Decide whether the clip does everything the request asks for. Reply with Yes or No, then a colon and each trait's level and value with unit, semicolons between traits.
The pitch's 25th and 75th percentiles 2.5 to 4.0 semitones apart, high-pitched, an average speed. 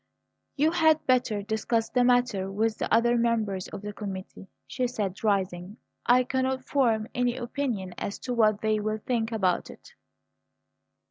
Yes: average, 3.3 semitones; high, 225 Hz; average, 155 wpm